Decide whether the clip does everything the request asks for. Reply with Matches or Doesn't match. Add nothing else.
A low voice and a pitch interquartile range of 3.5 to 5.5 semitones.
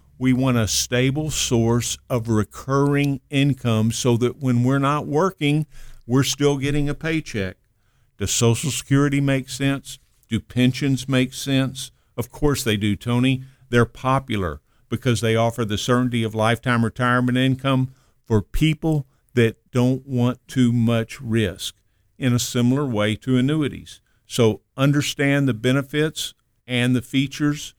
Doesn't match